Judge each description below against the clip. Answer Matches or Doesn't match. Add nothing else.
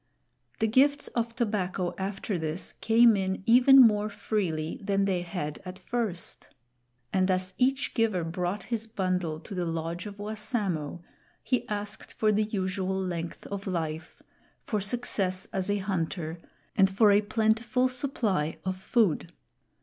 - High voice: Matches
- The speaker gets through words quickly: Doesn't match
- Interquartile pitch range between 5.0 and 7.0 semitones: Doesn't match